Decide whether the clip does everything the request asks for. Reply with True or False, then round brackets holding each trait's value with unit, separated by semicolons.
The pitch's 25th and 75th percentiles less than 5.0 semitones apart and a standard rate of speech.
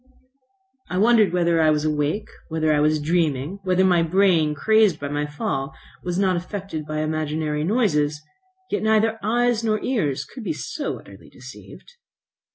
False (5.3 semitones; 160 wpm)